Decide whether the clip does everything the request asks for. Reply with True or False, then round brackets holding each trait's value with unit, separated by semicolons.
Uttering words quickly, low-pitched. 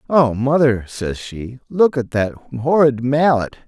False (145 wpm; 130 Hz)